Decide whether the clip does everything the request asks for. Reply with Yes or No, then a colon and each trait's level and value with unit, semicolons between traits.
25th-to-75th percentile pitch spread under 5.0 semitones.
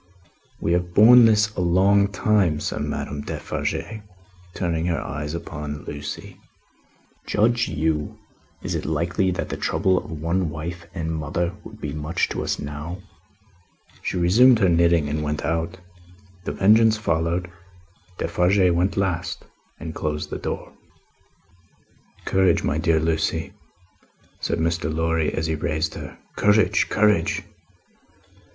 Yes: average, 3.4 semitones